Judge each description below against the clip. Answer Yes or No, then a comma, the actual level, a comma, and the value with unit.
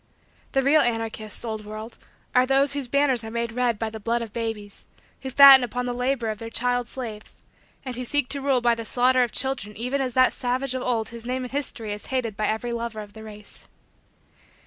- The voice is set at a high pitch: Yes, high, 240 Hz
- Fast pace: Yes, fast, 220 wpm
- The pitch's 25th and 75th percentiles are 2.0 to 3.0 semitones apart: Yes, narrow, 2.6 semitones